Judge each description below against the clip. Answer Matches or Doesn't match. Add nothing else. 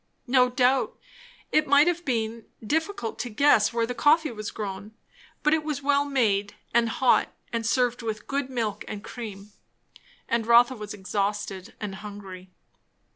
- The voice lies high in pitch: Matches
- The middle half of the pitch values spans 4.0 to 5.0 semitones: Matches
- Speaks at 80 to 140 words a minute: Doesn't match